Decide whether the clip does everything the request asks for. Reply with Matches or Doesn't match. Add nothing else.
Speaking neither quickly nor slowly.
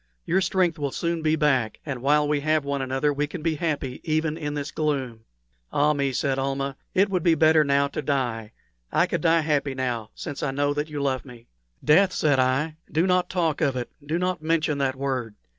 Doesn't match